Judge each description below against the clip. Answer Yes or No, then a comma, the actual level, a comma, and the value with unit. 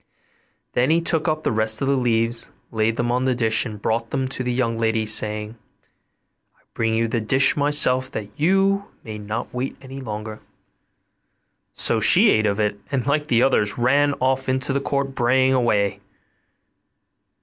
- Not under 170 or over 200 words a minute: Yes, average, 175 wpm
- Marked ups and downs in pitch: No, average, 3.4 semitones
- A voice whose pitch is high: No, low, 120 Hz